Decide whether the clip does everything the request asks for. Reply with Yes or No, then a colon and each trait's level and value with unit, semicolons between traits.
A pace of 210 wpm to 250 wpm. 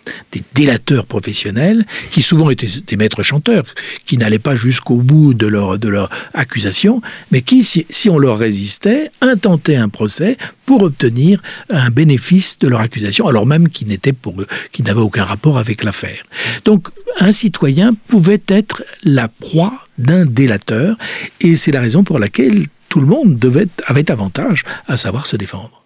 No: average, 170 wpm